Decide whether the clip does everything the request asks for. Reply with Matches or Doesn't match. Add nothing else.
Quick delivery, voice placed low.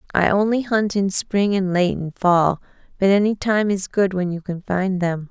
Doesn't match